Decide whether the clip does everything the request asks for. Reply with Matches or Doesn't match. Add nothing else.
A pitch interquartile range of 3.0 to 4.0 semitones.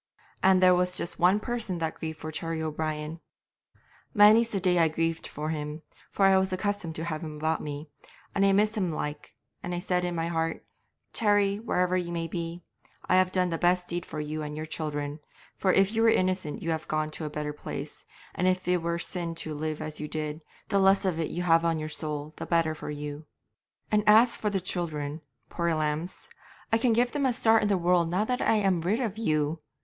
Matches